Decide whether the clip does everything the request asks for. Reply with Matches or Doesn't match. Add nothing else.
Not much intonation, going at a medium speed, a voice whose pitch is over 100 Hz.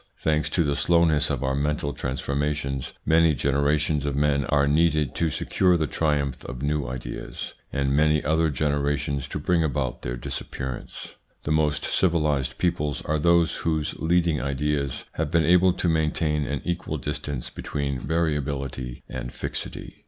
Doesn't match